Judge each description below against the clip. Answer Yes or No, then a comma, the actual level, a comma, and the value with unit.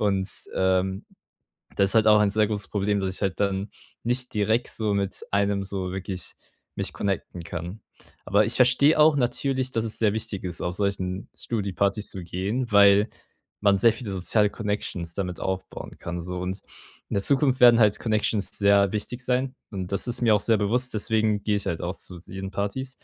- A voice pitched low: Yes, low, 100 Hz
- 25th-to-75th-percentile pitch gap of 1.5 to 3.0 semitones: Yes, average, 2.7 semitones